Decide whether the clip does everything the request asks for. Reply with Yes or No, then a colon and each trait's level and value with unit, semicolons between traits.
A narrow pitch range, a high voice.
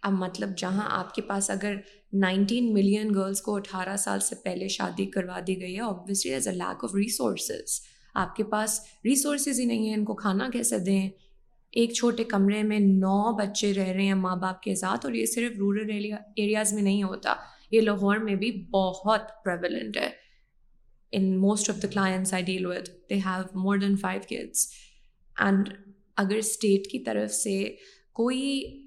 Yes: narrow, 2.1 semitones; high, 200 Hz